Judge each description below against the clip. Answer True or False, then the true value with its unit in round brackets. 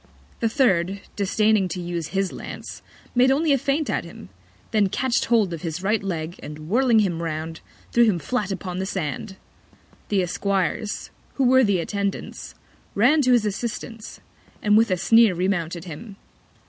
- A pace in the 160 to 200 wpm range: True (165 wpm)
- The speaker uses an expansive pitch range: False (4.7 semitones)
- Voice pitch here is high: True (200 Hz)